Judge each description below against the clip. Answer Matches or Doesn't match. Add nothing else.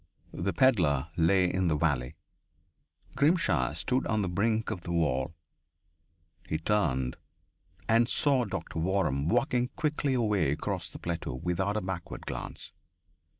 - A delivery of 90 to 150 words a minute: Matches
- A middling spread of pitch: Doesn't match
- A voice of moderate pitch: Doesn't match